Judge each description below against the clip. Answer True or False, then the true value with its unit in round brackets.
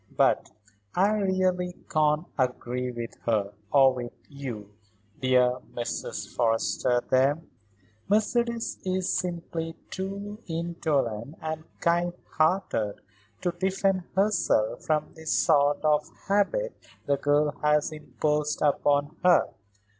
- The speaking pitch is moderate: True (155 Hz)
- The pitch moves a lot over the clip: True (5.9 semitones)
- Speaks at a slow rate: True (110 wpm)